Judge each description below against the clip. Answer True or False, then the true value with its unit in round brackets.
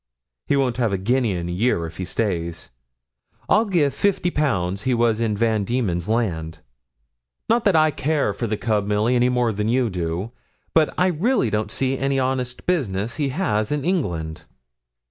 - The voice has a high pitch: False (115 Hz)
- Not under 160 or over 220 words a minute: True (185 wpm)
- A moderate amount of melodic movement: False (5.7 semitones)